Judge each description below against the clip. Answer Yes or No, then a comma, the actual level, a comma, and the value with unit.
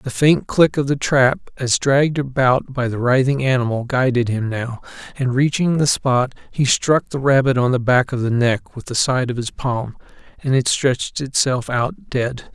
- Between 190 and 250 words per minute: Yes, average, 200 wpm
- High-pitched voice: No, low, 130 Hz